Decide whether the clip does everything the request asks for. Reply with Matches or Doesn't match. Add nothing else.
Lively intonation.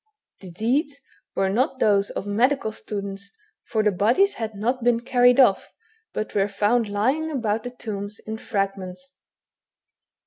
Doesn't match